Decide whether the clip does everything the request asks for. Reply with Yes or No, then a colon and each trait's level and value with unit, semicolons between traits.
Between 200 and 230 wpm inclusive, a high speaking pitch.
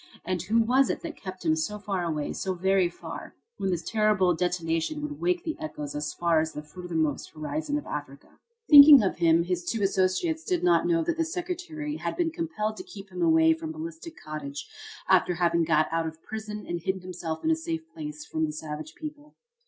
Yes: fast, 205 wpm; high, 195 Hz